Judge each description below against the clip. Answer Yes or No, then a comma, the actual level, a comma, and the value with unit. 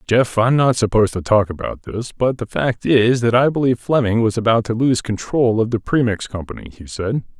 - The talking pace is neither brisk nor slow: No, fast, 220 wpm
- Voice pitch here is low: Yes, low, 115 Hz